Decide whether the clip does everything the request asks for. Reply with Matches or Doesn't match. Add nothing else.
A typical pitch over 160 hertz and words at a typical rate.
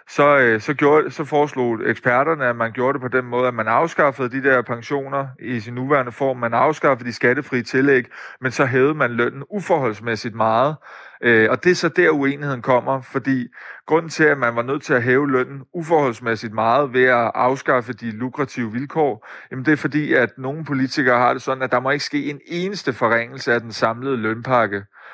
Doesn't match